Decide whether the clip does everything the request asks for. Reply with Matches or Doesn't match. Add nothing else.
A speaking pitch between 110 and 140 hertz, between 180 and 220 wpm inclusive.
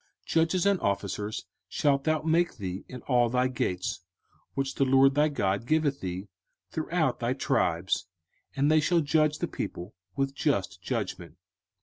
Doesn't match